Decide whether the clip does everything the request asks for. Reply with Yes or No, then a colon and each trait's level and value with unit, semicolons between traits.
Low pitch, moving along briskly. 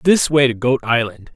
Yes: low, 130 Hz; fast, 220 wpm